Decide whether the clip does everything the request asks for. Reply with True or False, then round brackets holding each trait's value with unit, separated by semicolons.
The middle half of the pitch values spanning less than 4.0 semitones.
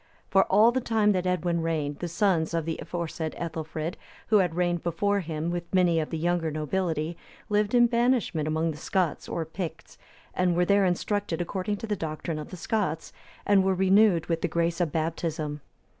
True (3.1 semitones)